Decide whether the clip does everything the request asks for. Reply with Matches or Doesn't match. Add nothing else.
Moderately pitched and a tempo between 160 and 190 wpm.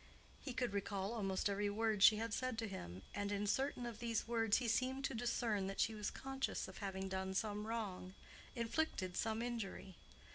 Doesn't match